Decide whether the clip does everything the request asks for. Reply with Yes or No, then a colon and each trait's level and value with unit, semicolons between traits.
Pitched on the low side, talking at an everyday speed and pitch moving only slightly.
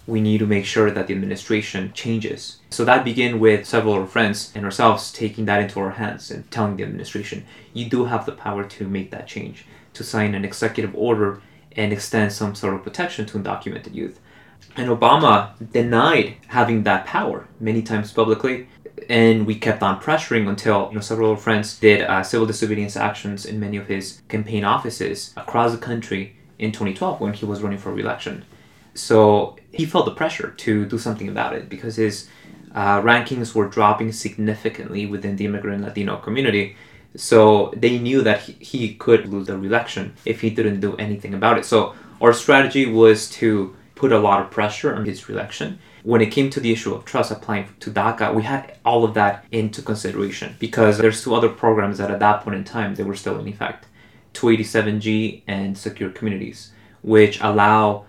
Yes: low, 110 Hz; average, 190 wpm; narrow, 1.9 semitones